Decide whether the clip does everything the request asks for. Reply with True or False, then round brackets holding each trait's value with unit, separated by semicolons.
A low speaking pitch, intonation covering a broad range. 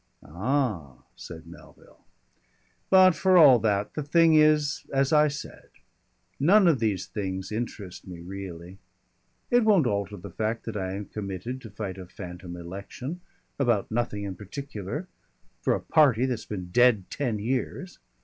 True (110 Hz; 7.0 semitones)